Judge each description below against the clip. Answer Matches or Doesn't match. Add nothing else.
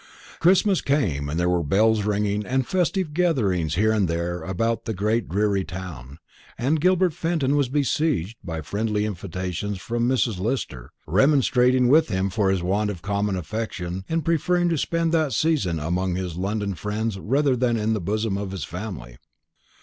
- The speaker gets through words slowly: Doesn't match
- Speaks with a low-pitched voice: Matches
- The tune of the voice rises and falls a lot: Matches